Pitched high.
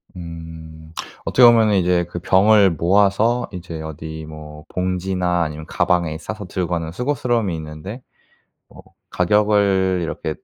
No: very low, 90 Hz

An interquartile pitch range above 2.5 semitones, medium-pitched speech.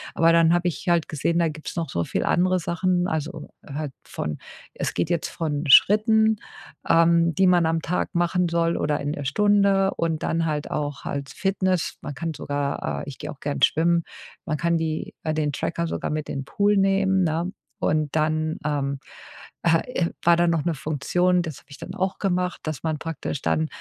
Yes: average, 2.9 semitones; medium, 165 Hz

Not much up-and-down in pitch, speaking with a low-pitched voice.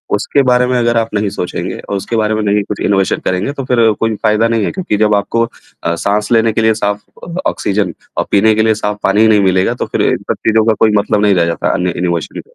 Yes: narrow, 1.9 semitones; low, 105 Hz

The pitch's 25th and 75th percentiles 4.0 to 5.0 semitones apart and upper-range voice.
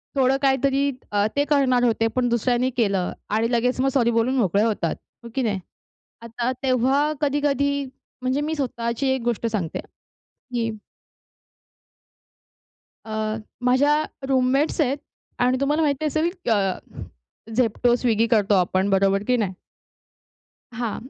No: average, 3.6 semitones; high, 245 Hz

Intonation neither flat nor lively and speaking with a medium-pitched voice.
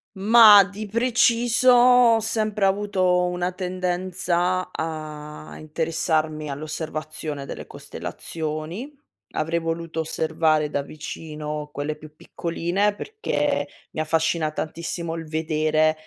Yes: average, 4.1 semitones; medium, 165 Hz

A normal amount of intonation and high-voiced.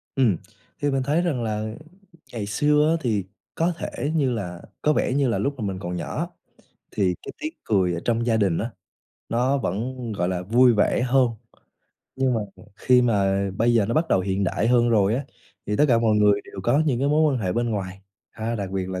No: average, 5.0 semitones; low, 115 Hz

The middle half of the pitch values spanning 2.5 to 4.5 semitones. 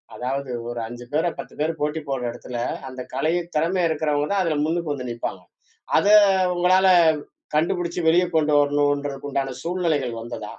Yes: average, 4.1 semitones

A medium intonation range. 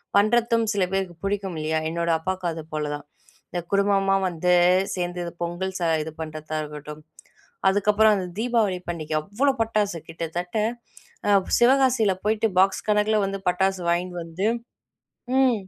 Yes: average, 3.7 semitones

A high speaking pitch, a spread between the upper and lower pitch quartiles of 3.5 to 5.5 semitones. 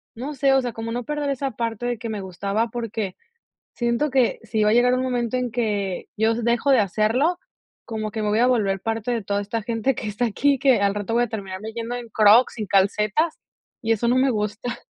No: high, 230 Hz; average, 2.7 semitones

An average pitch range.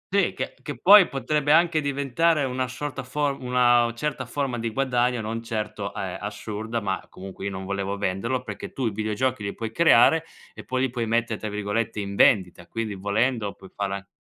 Yes: average, 4.4 semitones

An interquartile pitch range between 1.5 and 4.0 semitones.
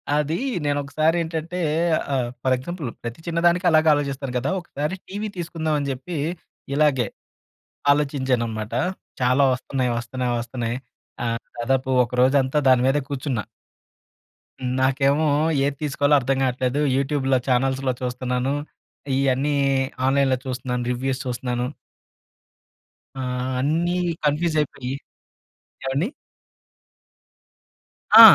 Yes: average, 2.8 semitones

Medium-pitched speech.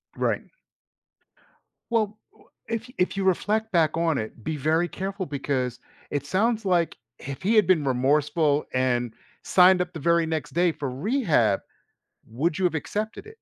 Yes: medium, 165 Hz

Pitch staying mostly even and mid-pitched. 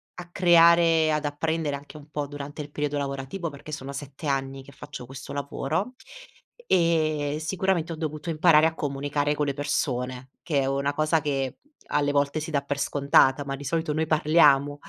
Yes: narrow, 2.1 semitones; medium, 145 Hz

